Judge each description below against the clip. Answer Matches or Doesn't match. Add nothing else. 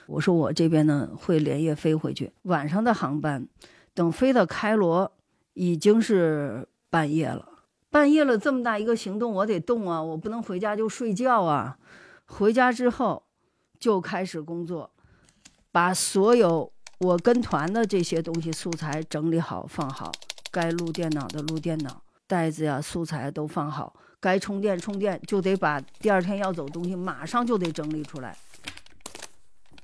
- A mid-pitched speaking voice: Matches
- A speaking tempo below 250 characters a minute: Matches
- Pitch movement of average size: Matches